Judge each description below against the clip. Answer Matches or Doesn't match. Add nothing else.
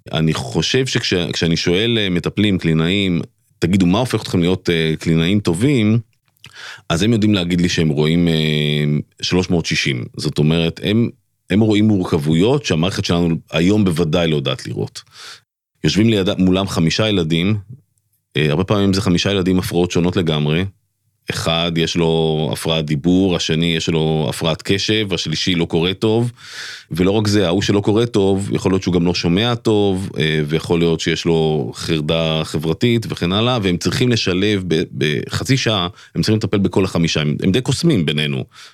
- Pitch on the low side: Matches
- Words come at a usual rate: Doesn't match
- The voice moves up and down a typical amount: Matches